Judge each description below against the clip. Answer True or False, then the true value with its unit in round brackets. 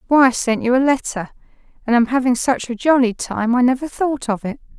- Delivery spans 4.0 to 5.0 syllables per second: False (5.5 syllables/s)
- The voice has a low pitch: False (250 Hz)